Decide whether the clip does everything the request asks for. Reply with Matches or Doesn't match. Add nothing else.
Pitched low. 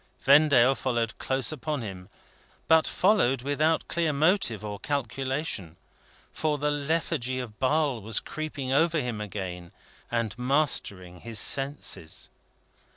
Matches